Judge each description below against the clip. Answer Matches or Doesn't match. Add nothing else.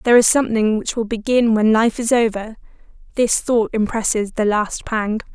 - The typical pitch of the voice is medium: Doesn't match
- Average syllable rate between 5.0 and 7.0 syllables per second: Matches